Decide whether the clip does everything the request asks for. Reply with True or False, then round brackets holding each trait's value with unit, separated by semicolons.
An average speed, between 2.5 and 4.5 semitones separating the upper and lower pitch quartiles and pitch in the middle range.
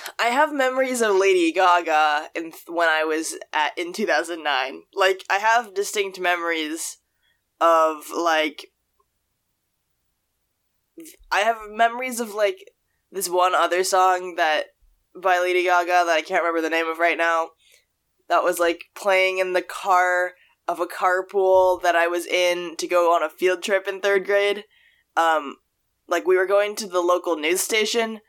True (160 wpm; 3.0 semitones; 180 Hz)